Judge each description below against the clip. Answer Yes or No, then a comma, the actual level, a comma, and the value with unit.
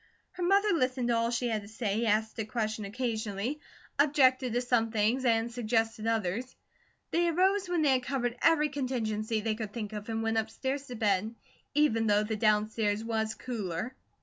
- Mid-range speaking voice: No, high, 230 Hz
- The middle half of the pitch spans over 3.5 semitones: No, average, 3.0 semitones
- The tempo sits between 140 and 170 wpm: No, average, 180 wpm